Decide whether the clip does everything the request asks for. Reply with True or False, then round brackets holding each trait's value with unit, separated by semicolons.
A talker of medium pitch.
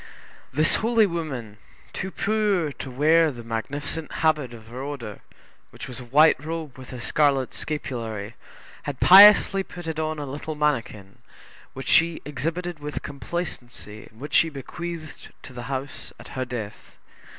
True (145 Hz)